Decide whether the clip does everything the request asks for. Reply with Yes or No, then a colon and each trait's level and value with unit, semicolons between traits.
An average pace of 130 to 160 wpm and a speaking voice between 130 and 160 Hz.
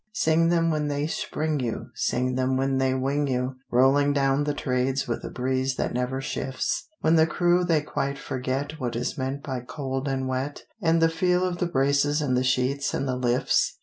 No: fast, 205 wpm; low, 135 Hz